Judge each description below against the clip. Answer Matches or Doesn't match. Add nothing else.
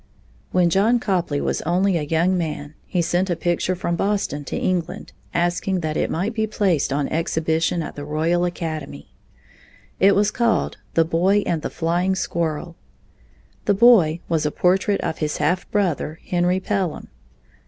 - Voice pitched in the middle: Matches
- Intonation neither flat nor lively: Matches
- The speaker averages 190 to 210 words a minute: Doesn't match